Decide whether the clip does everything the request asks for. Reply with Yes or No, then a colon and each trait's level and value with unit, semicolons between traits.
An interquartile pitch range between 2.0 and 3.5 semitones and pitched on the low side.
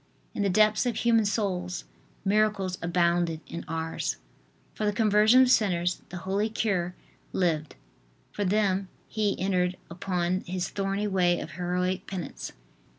No: average, 2.9 semitones; high, 190 Hz